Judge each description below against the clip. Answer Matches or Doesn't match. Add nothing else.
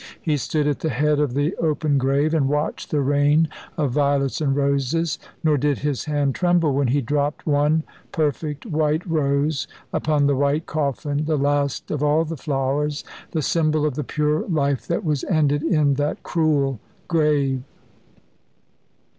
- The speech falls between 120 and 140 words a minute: Doesn't match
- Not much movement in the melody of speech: Matches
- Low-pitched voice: Doesn't match